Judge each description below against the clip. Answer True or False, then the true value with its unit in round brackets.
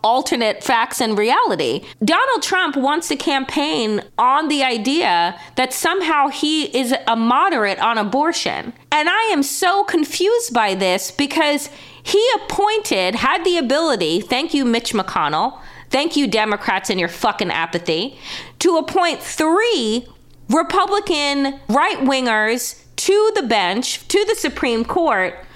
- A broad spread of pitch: True (7.0 semitones)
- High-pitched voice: True (285 Hz)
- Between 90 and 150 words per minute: True (135 wpm)